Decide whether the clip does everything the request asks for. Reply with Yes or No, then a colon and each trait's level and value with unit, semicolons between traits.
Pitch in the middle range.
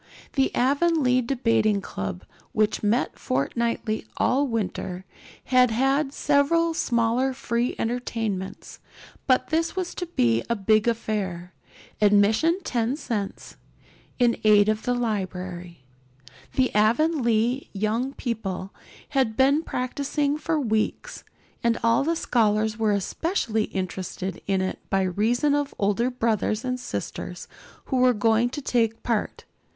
No: high, 230 Hz